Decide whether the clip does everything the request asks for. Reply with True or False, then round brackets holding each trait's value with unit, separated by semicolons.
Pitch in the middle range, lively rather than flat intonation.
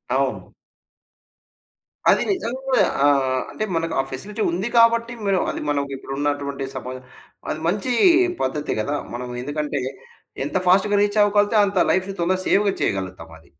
True (170 Hz; 6.6 semitones)